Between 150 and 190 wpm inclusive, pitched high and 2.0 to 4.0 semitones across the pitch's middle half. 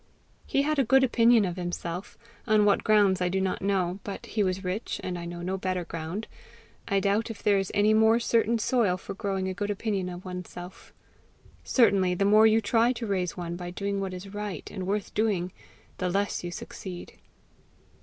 No: average, 200 wpm; high, 195 Hz; average, 2.9 semitones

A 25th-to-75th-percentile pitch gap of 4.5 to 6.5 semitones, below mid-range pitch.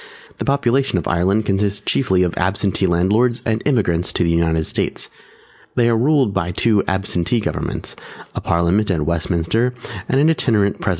Yes: average, 5.1 semitones; low, 100 Hz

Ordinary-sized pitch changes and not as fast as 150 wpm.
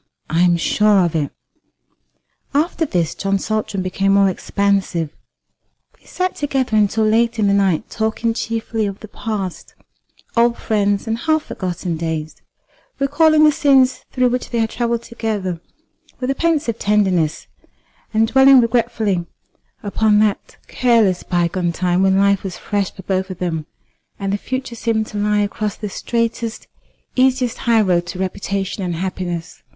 No: average, 3.9 semitones; average, 155 wpm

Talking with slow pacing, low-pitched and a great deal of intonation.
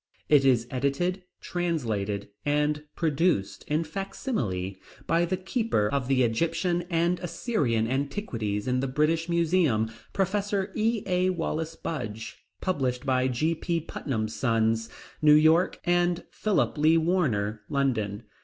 No: slow, 125 wpm; medium, 150 Hz; wide, 6.5 semitones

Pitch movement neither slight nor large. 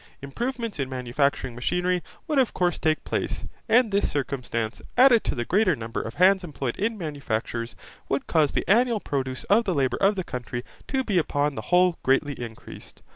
No: wide, 7.6 semitones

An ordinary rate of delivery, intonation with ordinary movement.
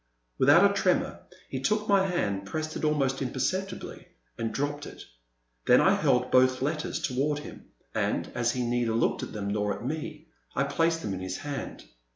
Yes: average, 185 wpm; average, 4.6 semitones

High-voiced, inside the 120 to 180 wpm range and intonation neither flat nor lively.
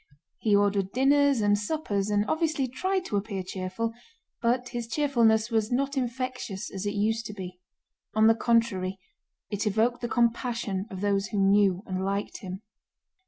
Yes: high, 220 Hz; average, 165 wpm; average, 3.5 semitones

